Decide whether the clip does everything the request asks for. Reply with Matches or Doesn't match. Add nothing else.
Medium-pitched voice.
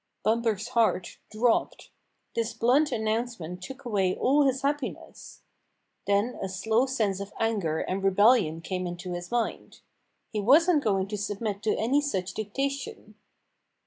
Doesn't match